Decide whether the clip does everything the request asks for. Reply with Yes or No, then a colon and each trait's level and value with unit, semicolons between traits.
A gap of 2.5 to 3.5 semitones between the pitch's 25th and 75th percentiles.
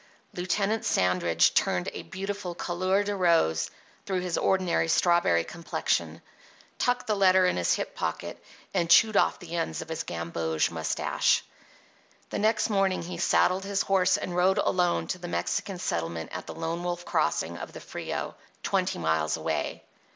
Yes: average, 3.1 semitones